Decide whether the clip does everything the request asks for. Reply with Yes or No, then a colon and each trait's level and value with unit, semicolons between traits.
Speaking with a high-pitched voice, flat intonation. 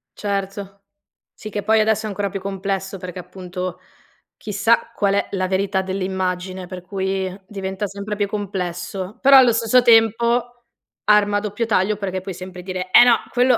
Yes: high, 195 Hz; narrow, 2.3 semitones